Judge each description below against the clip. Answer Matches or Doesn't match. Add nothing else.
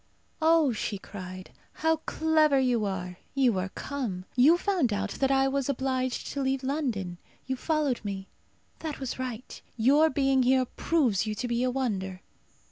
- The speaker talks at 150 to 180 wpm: Matches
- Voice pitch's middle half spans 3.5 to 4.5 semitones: Doesn't match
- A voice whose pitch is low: Doesn't match